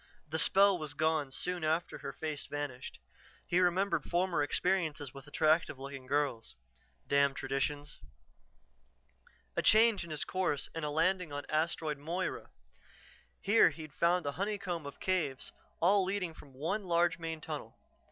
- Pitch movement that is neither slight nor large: Yes, average, 3.9 semitones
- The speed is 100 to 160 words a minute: Yes, average, 145 wpm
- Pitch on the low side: No, medium, 160 Hz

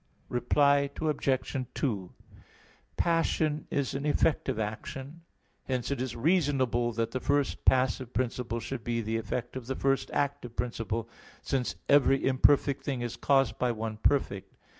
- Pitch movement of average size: Yes, average, 3.2 semitones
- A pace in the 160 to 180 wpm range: No, average, 145 wpm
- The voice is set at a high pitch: No, low, 130 Hz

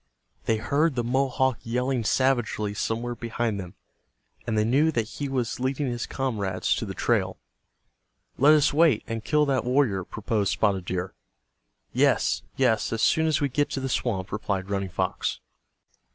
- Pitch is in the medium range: No, low, 120 Hz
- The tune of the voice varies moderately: Yes, average, 4.2 semitones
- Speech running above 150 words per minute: Yes, average, 165 wpm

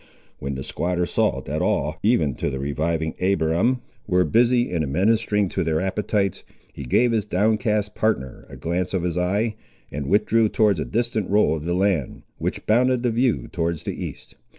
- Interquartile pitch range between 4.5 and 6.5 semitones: Yes, average, 5.1 semitones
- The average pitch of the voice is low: Yes, very low, 95 Hz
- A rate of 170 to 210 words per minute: Yes, average, 180 wpm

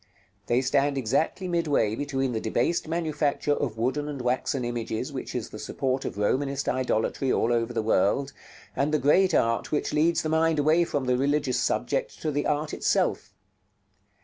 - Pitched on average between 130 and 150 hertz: Yes, medium, 140 Hz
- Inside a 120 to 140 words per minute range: No, average, 175 wpm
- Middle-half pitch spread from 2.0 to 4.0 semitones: Yes, average, 3.6 semitones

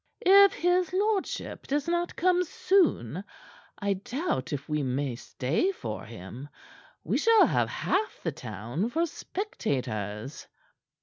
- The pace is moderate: No, slow, 125 wpm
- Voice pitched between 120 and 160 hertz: No, high, 235 Hz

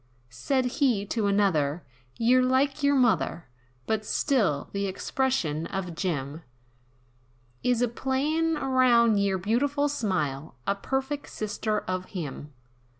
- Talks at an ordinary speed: No, slow, 120 wpm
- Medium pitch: No, high, 220 Hz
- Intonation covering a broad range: Yes, wide, 6.2 semitones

